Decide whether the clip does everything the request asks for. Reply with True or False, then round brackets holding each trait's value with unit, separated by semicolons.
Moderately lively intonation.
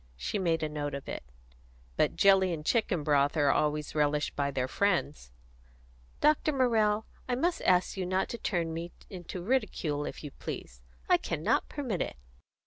False (6.0 semitones)